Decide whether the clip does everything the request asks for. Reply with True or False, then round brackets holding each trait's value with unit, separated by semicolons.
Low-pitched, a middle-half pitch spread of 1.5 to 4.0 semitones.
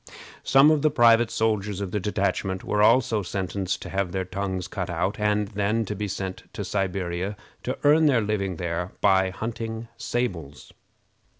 True (100 Hz; 3.1 semitones)